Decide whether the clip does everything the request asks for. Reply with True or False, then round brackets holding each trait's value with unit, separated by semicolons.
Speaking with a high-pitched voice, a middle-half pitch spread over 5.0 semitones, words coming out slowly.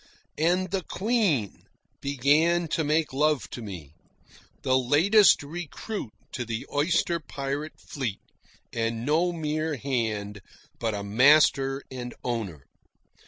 False (140 Hz; 5.6 semitones; 120 wpm)